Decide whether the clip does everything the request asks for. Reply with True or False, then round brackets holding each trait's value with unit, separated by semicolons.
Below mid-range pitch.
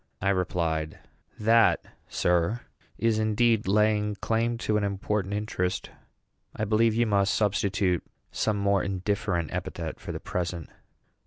True (105 Hz)